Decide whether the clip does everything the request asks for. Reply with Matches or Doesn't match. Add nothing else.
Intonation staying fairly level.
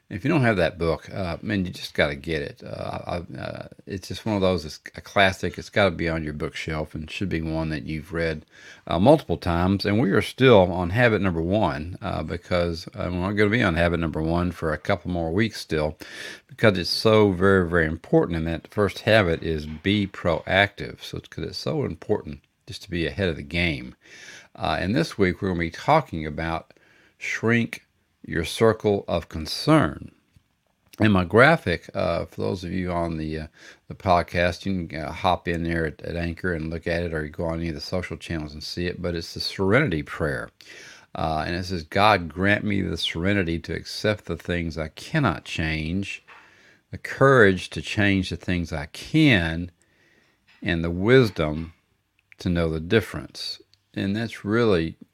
Doesn't match